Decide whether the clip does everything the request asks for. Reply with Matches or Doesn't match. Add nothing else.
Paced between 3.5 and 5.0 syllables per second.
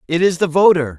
Doesn't match